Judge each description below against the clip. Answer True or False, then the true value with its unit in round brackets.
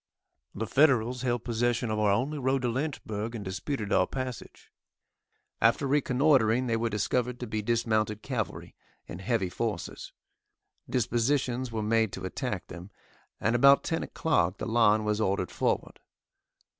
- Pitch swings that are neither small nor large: True (3.1 semitones)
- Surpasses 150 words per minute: False (145 wpm)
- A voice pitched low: True (115 Hz)